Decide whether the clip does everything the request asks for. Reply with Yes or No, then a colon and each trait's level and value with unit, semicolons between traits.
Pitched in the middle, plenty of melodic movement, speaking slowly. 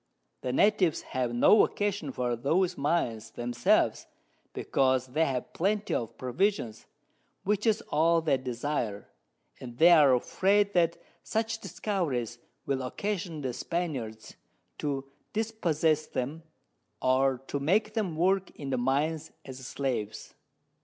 Yes: medium, 150 Hz; wide, 6.4 semitones; slow, 125 wpm